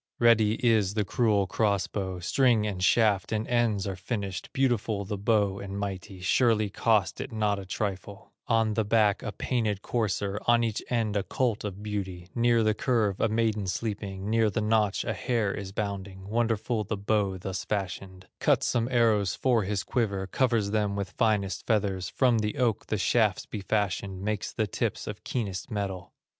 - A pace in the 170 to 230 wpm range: Yes, average, 180 wpm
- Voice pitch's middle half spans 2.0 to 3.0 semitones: Yes, narrow, 2.4 semitones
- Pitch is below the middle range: Yes, low, 105 Hz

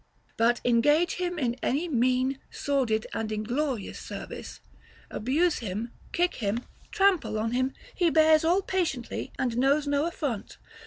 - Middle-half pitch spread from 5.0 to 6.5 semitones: Yes, average, 5.3 semitones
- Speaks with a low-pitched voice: No, very high, 270 Hz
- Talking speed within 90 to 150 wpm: Yes, average, 140 wpm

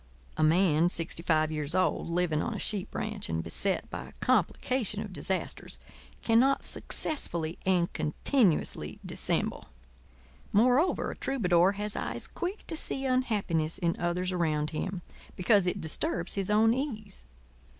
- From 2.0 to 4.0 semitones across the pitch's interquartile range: No, average, 5.0 semitones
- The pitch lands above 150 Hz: Yes, medium, 185 Hz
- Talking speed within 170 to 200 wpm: No, average, 140 wpm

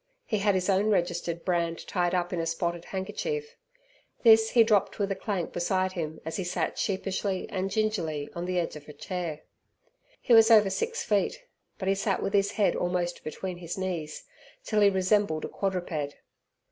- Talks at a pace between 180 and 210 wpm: Yes, average, 185 wpm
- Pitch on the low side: No, medium, 185 Hz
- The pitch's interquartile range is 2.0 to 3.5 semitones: Yes, average, 2.9 semitones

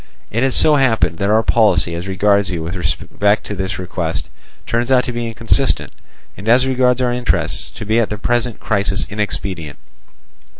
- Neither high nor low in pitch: No, low, 105 Hz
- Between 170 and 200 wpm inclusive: Yes, average, 180 wpm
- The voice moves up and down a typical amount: Yes, average, 4.3 semitones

